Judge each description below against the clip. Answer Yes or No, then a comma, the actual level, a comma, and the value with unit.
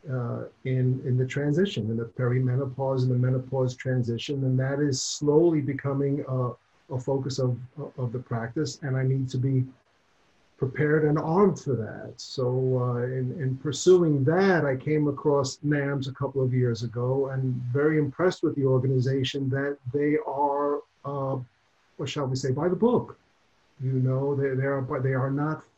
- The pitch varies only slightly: Yes, narrow, 2.0 semitones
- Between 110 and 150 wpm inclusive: No, average, 170 wpm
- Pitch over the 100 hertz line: Yes, low, 135 Hz